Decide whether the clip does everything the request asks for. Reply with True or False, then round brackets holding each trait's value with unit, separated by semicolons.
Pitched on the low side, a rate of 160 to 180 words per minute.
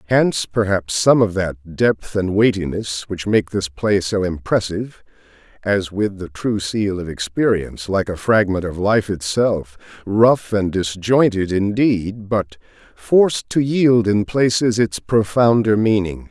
False (100 Hz; 145 wpm)